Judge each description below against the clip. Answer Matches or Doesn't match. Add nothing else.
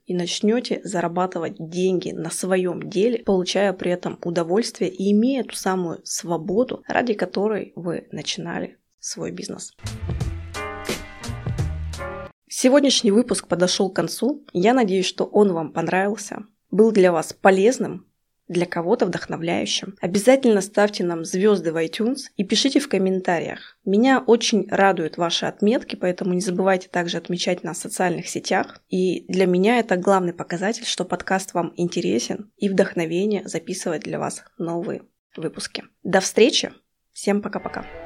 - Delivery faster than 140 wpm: Doesn't match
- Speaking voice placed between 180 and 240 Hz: Matches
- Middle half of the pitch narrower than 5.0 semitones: Matches